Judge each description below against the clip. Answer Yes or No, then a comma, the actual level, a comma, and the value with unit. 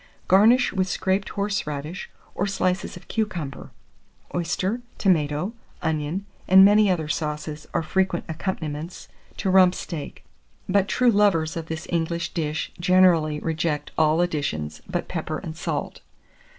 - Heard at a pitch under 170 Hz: No, medium, 175 Hz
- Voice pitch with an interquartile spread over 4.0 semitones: No, average, 3.5 semitones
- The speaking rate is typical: No, slow, 130 wpm